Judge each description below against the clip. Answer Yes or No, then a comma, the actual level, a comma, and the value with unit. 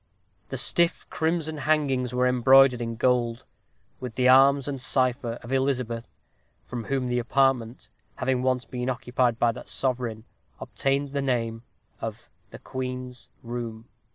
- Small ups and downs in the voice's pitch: Yes, narrow, 2.0 semitones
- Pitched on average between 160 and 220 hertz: No, low, 125 Hz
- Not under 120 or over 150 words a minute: Yes, average, 140 wpm